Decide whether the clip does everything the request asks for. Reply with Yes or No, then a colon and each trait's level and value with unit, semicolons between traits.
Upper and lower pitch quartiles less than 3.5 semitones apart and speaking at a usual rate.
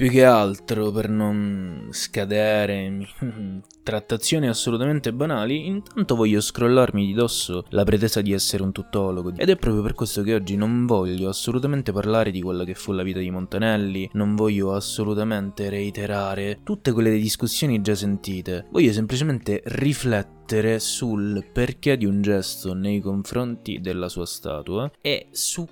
Yes: average, 3.0 semitones; average, 145 wpm